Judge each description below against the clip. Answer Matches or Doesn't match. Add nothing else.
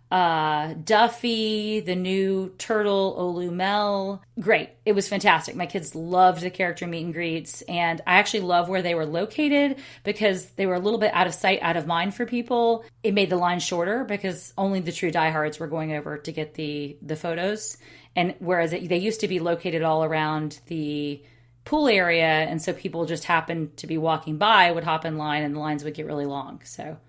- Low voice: Doesn't match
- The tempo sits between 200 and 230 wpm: Matches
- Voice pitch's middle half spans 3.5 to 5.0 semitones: Matches